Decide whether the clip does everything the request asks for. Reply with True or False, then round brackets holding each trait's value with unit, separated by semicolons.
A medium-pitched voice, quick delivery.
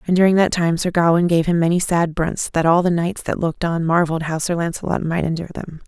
True (170 Hz; 255 wpm)